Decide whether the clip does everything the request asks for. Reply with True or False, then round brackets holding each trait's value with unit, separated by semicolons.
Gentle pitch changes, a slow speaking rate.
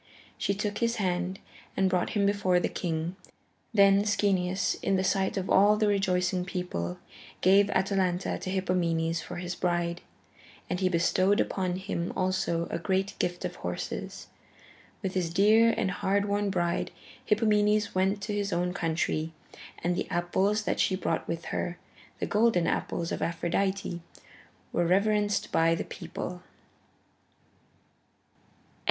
False (2.3 semitones; 145 wpm)